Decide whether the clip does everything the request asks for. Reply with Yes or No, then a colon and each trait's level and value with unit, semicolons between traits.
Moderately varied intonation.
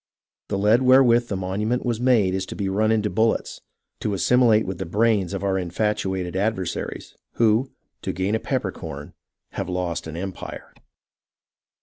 Yes: average, 3.2 semitones